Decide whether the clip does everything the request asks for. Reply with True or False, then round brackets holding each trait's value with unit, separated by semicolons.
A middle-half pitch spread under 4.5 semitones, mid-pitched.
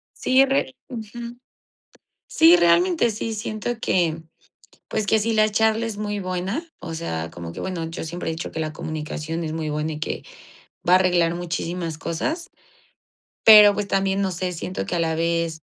False (4.8 semitones; 180 Hz)